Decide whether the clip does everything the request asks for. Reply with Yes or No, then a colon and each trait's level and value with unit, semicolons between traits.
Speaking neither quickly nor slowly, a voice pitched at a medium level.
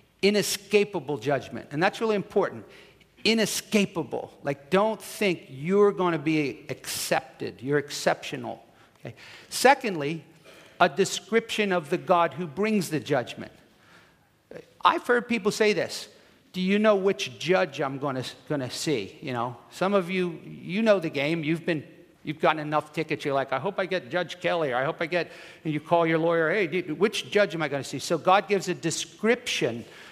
Yes: average, 180 wpm; medium, 170 Hz